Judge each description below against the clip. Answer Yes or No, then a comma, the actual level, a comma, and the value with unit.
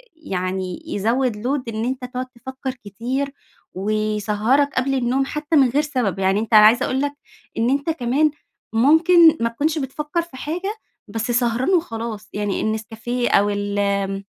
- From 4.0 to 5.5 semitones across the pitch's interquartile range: Yes, average, 4.8 semitones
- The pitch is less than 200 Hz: No, high, 245 Hz